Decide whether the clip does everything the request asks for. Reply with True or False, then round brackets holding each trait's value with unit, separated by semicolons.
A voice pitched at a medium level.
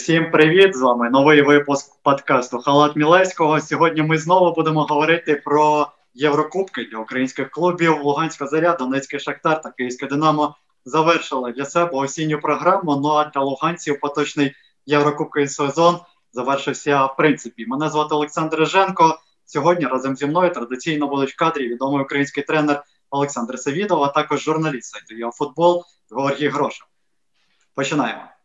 True (150 Hz)